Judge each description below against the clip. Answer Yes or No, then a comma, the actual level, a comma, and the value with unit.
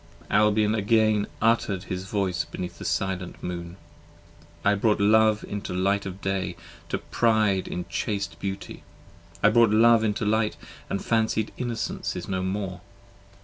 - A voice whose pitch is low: Yes, low, 100 Hz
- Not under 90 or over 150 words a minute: Yes, average, 145 wpm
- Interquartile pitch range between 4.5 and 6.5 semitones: No, narrow, 2.6 semitones